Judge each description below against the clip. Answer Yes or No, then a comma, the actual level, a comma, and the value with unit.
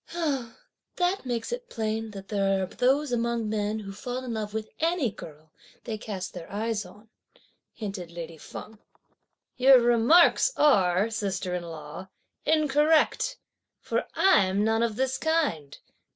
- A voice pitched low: No, high, 220 Hz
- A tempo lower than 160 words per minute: Yes, average, 140 wpm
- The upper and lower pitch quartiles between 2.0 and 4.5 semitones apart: No, average, 5.0 semitones